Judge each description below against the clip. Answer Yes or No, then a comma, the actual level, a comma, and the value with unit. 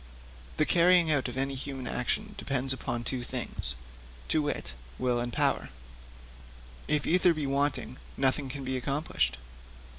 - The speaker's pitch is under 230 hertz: Yes, low, 135 Hz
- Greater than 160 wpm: No, average, 145 wpm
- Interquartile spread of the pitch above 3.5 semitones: No, average, 3.0 semitones